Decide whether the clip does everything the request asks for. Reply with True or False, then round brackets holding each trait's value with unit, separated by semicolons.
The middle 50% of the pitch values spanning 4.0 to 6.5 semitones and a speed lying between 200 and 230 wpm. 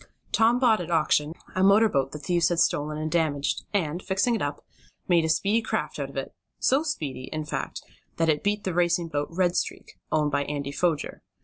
True (4.5 semitones; 205 wpm)